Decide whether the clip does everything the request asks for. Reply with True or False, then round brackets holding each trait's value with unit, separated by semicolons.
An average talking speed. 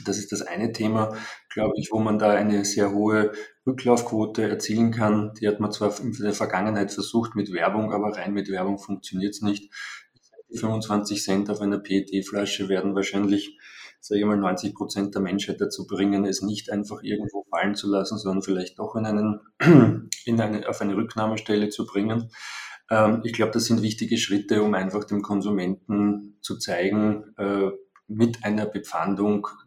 True (170 wpm)